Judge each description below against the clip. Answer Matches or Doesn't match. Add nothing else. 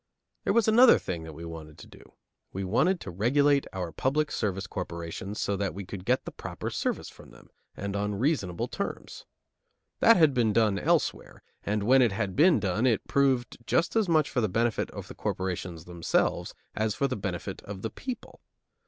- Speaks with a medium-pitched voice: Doesn't match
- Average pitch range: Doesn't match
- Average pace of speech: Matches